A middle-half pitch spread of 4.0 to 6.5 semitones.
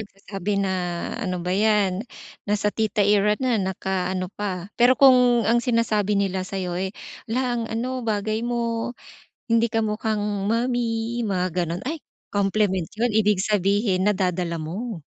No: average, 3.3 semitones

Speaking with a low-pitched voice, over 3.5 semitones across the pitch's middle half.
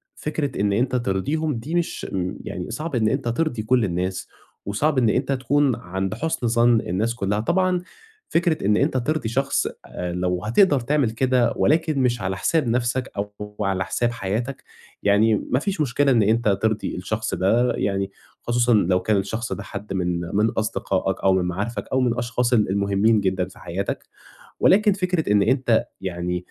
Yes: low, 115 Hz; average, 4.9 semitones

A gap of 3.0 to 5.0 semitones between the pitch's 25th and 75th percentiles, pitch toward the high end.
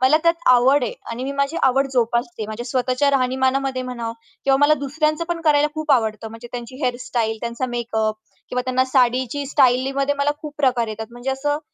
No: narrow, 2.6 semitones; very high, 255 Hz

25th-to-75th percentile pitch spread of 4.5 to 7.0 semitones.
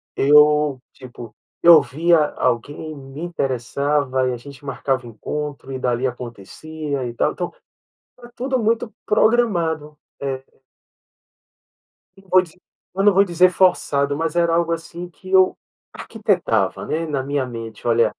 Yes: average, 4.9 semitones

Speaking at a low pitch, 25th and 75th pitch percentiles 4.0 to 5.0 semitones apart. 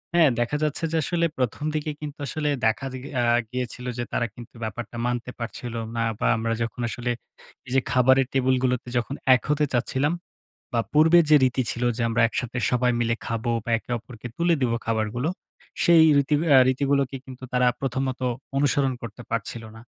No: low, 125 Hz; average, 2.8 semitones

